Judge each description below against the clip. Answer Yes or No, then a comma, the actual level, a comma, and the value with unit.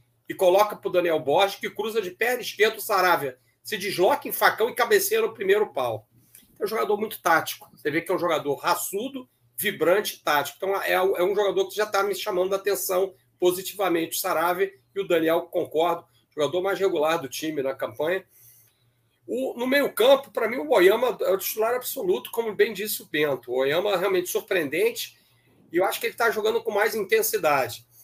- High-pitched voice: Yes, high, 195 Hz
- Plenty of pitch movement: Yes, wide, 7.4 semitones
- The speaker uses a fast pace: Yes, fast, 195 wpm